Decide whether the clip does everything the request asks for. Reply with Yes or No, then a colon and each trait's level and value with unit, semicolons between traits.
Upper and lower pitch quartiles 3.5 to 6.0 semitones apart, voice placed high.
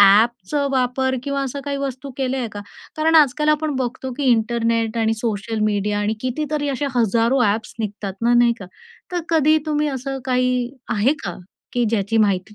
Yes: average, 3.9 semitones; high, 245 Hz